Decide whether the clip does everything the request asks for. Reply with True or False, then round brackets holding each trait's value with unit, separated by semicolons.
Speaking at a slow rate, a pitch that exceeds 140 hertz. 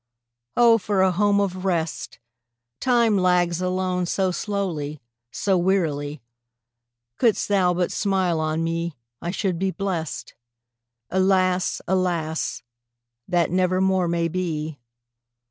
True (115 wpm; 185 Hz)